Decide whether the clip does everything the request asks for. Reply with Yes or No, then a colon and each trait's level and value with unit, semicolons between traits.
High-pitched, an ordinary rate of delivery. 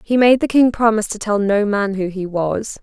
No: high, 210 Hz; fast, 255 wpm